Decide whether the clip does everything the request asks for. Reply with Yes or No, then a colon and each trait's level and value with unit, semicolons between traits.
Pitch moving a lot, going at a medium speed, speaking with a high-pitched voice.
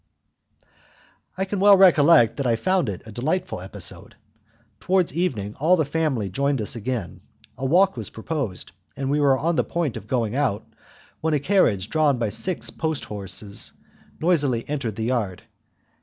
No: wide, 6.9 semitones; average, 165 wpm; low, 135 Hz